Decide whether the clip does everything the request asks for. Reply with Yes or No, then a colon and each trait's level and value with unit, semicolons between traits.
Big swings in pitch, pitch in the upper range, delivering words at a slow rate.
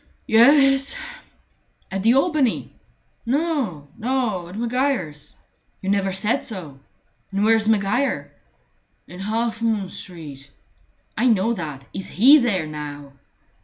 Yes: wide, 5.7 semitones; high, 215 Hz; slow, 125 wpm